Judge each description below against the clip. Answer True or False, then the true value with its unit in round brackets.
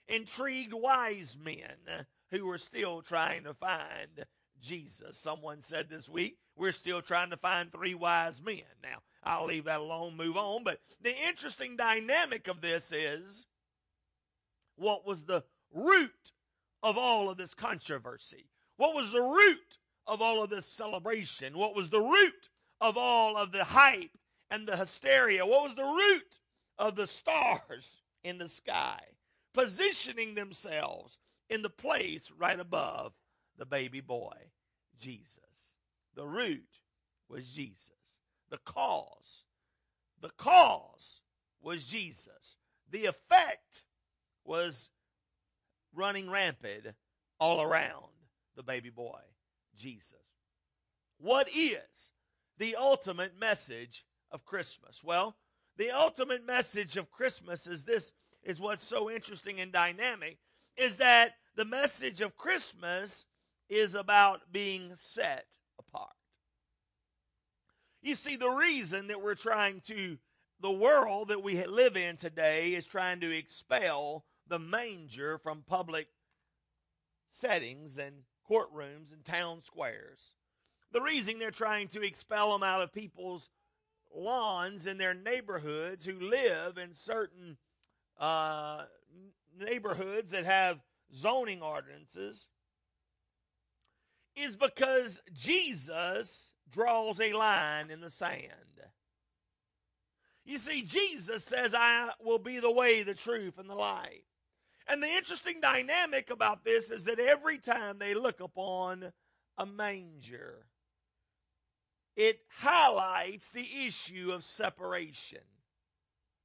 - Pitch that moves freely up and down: True (6.8 semitones)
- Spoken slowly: True (120 wpm)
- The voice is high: True (195 Hz)